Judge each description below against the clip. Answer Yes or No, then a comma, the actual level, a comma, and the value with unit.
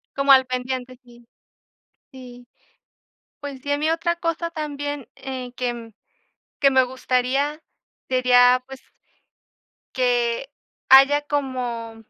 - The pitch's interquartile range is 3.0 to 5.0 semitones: No, narrow, 2.6 semitones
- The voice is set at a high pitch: Yes, very high, 260 Hz